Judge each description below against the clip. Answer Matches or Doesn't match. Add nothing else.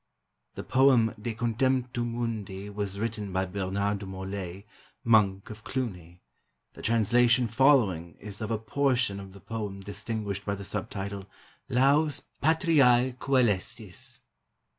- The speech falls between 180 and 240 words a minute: Doesn't match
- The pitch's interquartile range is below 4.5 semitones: Matches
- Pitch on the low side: Matches